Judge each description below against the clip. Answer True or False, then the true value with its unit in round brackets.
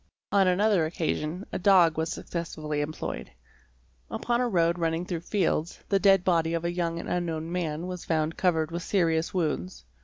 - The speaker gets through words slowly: False (180 wpm)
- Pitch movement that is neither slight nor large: False (2.1 semitones)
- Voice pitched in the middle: True (170 Hz)